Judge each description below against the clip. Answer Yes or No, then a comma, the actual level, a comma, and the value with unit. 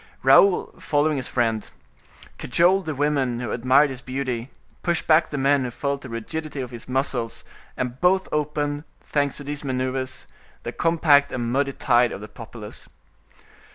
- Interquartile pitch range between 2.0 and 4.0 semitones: Yes, average, 3.0 semitones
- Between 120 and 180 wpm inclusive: Yes, average, 160 wpm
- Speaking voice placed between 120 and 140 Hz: Yes, low, 135 Hz